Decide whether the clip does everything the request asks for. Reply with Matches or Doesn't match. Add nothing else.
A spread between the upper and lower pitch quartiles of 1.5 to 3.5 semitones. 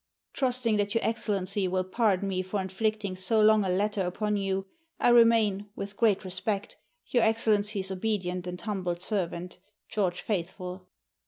Matches